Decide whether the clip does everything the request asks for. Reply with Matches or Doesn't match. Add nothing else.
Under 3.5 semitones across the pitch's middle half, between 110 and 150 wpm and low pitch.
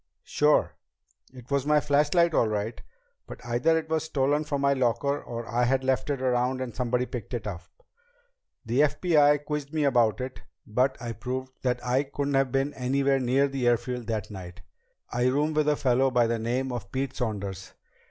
Doesn't match